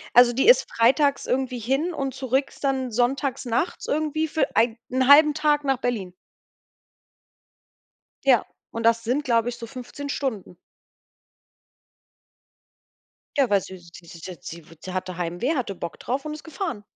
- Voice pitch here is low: No, very high, 250 Hz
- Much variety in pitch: No, average, 4.1 semitones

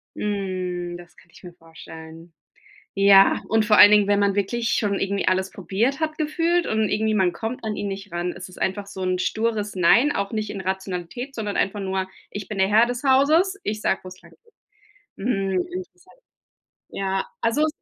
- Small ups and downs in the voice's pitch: No, average, 3.0 semitones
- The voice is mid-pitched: No, high, 200 Hz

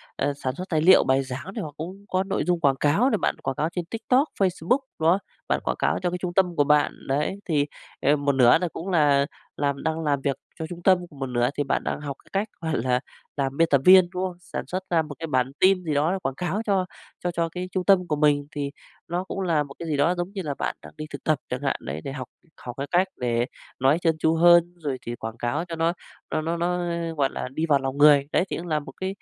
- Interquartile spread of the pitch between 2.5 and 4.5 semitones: Yes, average, 4.1 semitones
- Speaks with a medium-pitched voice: Yes, medium, 160 Hz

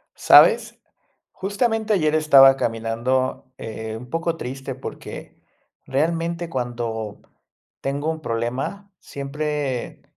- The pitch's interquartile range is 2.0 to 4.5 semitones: No, average, 5.2 semitones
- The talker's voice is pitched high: No, low, 135 Hz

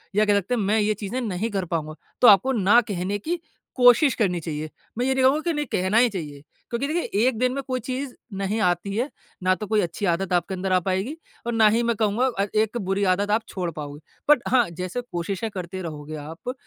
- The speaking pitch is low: No, high, 205 Hz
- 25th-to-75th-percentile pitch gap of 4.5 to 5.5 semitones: Yes, average, 4.9 semitones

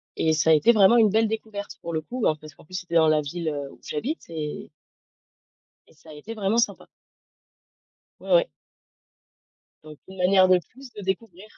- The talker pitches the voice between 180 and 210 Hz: Yes, medium, 185 Hz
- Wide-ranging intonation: Yes, wide, 5.7 semitones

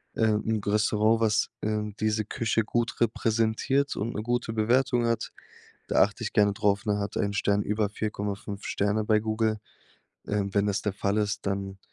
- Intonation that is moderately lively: No, narrow, 1.6 semitones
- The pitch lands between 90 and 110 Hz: Yes, low, 105 Hz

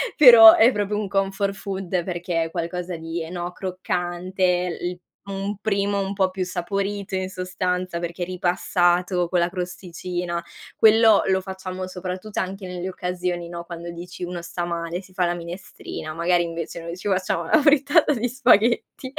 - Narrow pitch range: Yes, narrow, 2.0 semitones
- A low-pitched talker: No, medium, 185 Hz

